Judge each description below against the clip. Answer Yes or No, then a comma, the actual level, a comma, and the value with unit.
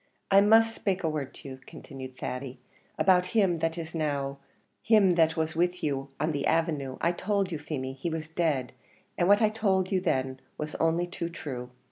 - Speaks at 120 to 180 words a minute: No, average, 195 wpm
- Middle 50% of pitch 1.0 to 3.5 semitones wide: No, average, 4.7 semitones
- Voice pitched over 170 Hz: No, medium, 165 Hz